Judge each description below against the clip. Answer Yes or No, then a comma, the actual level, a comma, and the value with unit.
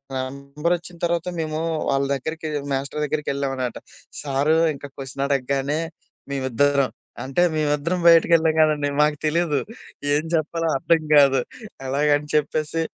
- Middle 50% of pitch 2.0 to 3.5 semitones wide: Yes, narrow, 2.4 semitones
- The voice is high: No, medium, 150 Hz